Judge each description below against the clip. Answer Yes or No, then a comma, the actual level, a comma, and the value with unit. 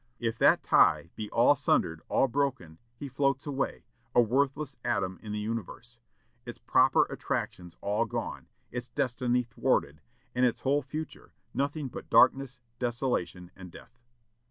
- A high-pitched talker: No, low, 120 Hz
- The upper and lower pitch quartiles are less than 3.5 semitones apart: No, average, 4.5 semitones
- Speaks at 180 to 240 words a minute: No, average, 145 wpm